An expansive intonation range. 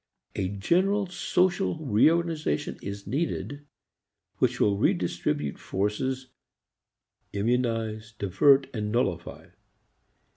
Yes: wide, 7.2 semitones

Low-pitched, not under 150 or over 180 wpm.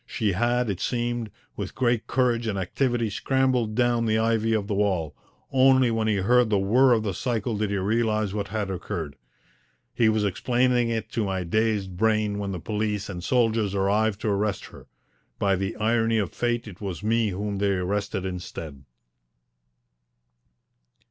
Yes: low, 110 Hz; average, 170 wpm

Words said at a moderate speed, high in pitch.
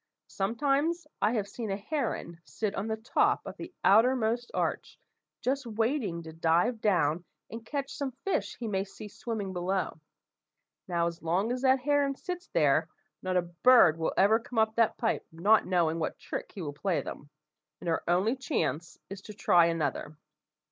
Yes: average, 175 wpm; high, 210 Hz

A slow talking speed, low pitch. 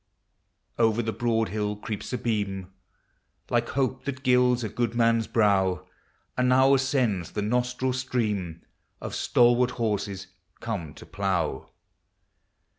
Yes: slow, 125 wpm; low, 115 Hz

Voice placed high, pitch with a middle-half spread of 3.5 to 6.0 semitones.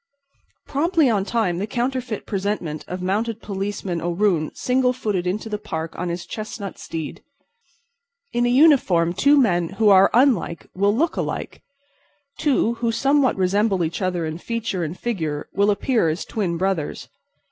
Yes: high, 200 Hz; average, 5.2 semitones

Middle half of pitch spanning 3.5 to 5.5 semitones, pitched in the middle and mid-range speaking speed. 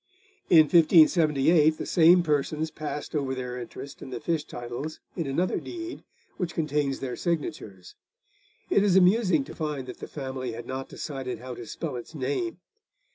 Yes: average, 4.2 semitones; medium, 150 Hz; average, 165 wpm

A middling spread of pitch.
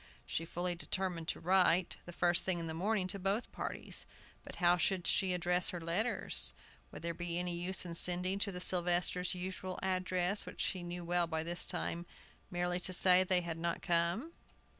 No: narrow, 1.2 semitones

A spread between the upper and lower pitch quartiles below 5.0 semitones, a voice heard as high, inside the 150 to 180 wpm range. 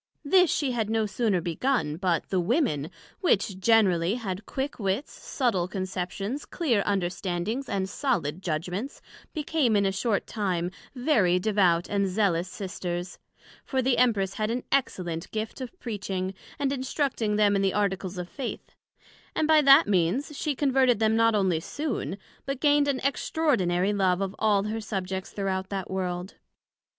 No: average, 5.3 semitones; high, 205 Hz; average, 155 wpm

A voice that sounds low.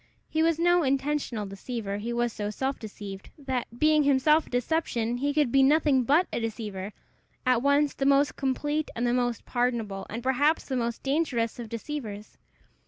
No: very high, 255 Hz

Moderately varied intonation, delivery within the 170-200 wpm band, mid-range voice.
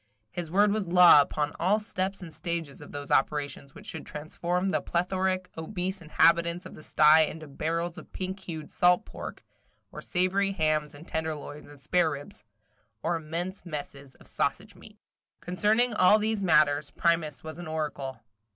No: average, 3.4 semitones; average, 160 wpm; medium, 170 Hz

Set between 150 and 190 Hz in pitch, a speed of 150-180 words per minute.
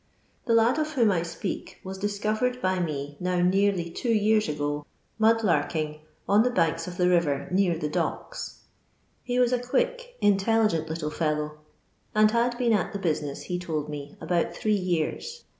Yes: medium, 185 Hz; average, 175 wpm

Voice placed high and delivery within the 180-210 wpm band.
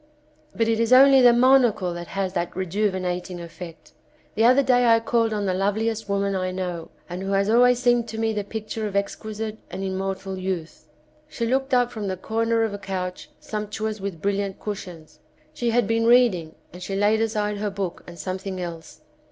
Yes: high, 205 Hz; average, 195 wpm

